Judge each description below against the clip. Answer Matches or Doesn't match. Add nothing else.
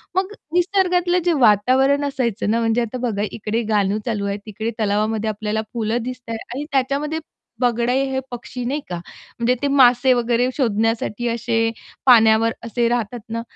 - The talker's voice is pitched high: Matches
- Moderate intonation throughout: Matches